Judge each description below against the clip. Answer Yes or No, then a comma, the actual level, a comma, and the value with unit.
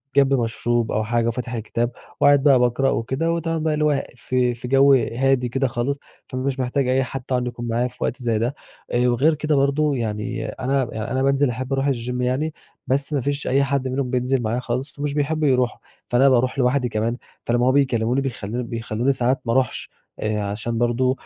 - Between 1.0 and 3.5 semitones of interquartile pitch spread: Yes, narrow, 2.5 semitones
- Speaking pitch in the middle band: No, low, 130 Hz